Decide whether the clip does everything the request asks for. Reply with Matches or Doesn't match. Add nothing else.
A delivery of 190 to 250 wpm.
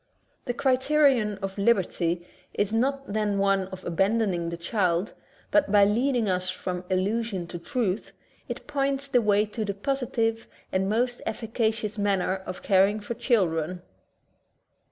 Doesn't match